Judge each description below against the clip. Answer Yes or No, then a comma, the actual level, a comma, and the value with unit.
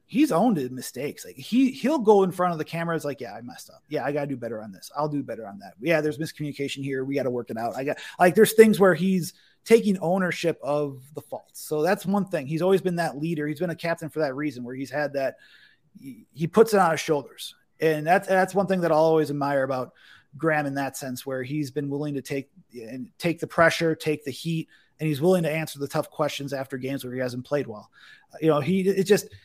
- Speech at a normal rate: No, fast, 255 wpm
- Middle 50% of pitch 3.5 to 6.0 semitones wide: Yes, average, 4.5 semitones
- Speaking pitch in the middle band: Yes, medium, 155 Hz